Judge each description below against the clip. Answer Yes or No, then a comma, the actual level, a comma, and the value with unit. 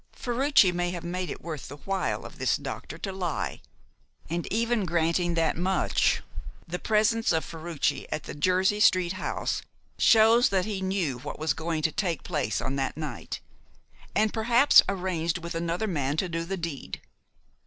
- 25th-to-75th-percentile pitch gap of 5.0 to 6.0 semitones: No, average, 3.4 semitones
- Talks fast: No, average, 170 wpm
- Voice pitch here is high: No, medium, 175 Hz